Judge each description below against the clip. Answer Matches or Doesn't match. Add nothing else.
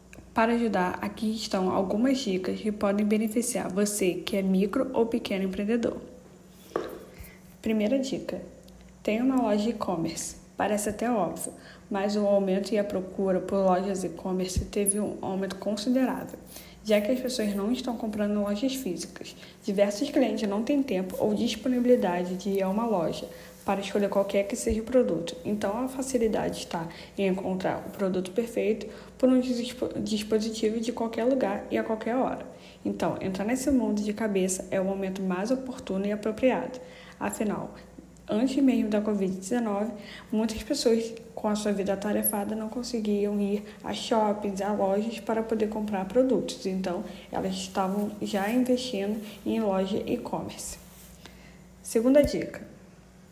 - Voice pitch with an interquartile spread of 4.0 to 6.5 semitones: Doesn't match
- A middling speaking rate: Matches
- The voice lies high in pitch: Matches